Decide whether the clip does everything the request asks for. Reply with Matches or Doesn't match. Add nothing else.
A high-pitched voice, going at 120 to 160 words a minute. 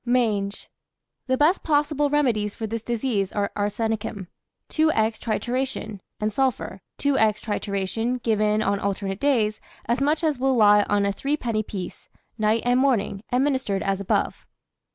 Matches